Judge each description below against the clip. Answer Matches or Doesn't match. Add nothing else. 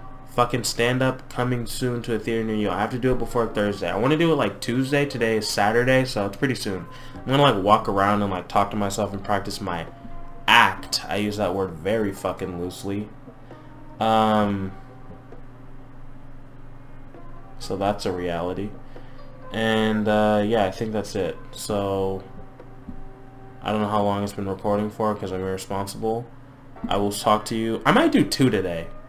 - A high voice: Doesn't match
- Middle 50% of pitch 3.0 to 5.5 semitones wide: Matches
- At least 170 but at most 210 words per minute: Matches